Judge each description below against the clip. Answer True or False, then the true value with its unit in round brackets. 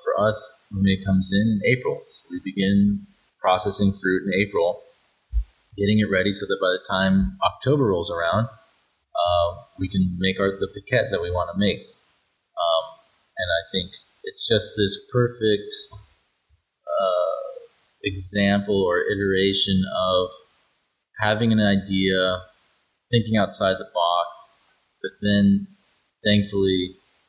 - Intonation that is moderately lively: False (2.3 semitones)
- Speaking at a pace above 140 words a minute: False (135 wpm)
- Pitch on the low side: True (100 Hz)